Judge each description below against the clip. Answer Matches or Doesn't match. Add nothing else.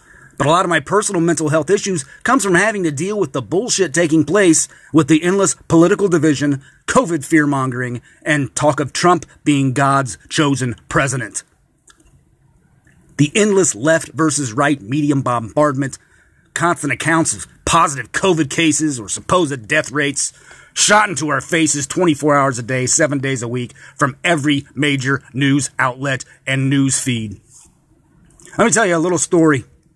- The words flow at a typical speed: Matches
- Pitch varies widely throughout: Doesn't match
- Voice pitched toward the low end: Doesn't match